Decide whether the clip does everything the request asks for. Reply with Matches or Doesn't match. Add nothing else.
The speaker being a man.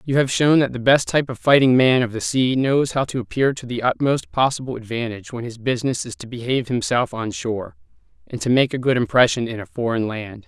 Matches